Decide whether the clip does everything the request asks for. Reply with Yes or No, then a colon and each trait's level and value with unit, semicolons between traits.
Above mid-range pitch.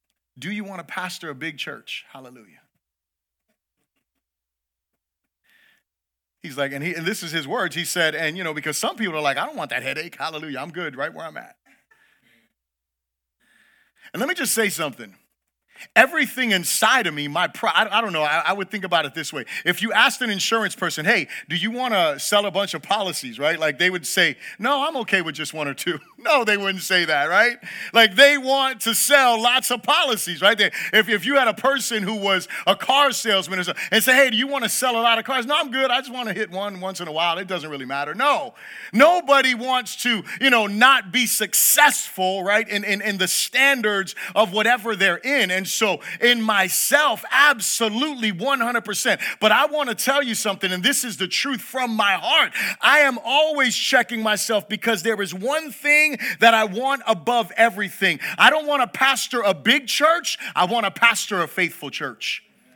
Yes: high, 215 Hz